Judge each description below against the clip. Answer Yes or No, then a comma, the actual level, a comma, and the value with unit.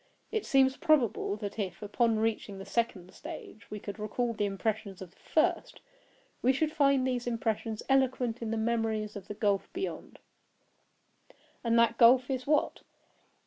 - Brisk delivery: No, average, 150 wpm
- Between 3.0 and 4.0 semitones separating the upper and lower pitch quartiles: Yes, average, 3.7 semitones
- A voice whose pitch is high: Yes, high, 230 Hz